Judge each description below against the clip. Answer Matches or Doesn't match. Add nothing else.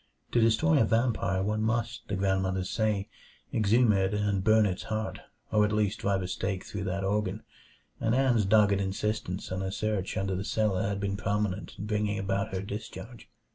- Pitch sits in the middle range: Doesn't match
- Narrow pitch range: Matches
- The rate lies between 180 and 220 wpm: Matches